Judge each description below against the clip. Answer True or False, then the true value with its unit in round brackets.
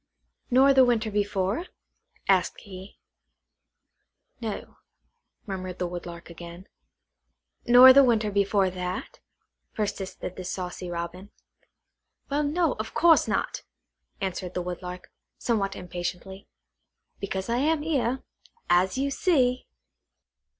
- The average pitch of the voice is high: True (200 Hz)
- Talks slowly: True (110 wpm)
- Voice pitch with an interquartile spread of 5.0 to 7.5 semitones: True (5.5 semitones)